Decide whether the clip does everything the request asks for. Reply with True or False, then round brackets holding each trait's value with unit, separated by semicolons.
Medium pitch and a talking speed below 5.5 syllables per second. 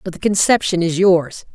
True (180 Hz; 5.1 syllables/s)